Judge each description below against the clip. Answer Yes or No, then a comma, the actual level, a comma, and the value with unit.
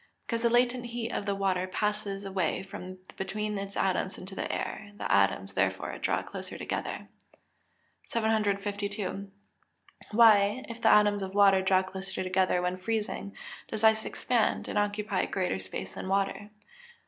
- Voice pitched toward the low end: No, high, 200 Hz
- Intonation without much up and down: Yes, narrow, 2.1 semitones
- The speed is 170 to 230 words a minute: No, average, 155 wpm